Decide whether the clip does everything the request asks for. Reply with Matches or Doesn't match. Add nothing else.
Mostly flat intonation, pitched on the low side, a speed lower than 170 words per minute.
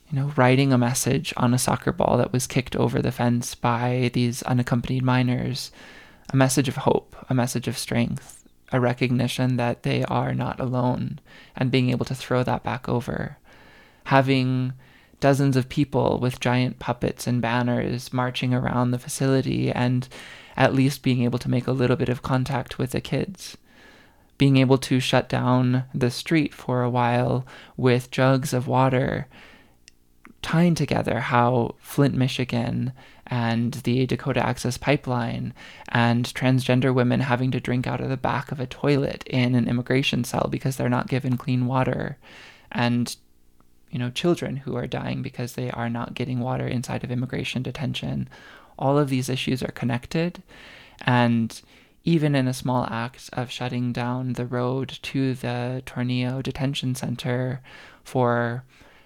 Matches